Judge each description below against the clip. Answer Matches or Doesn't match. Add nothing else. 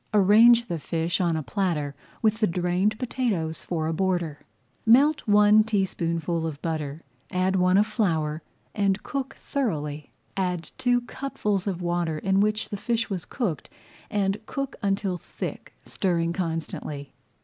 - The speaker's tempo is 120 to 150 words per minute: Matches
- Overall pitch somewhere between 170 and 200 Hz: Matches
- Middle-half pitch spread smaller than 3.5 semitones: Doesn't match